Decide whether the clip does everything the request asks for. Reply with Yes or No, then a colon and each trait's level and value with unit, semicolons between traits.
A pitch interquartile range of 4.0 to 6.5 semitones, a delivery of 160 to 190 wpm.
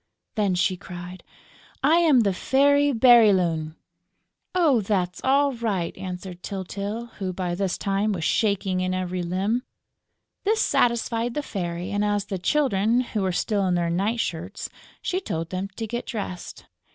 No: average, 4.5 semitones; average, 150 wpm